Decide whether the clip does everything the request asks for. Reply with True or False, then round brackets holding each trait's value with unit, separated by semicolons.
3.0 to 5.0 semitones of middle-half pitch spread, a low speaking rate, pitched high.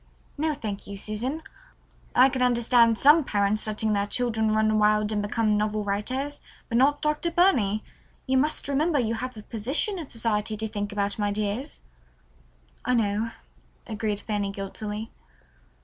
False (3.7 semitones; 155 wpm; 220 Hz)